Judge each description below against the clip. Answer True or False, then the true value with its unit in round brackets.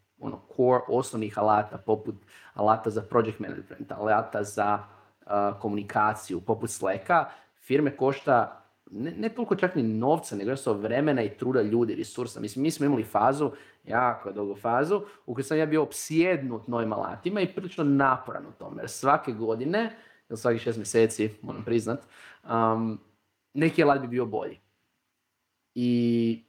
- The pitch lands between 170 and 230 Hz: False (120 Hz)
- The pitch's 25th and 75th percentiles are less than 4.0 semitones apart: False (4.8 semitones)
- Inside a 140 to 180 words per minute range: True (155 wpm)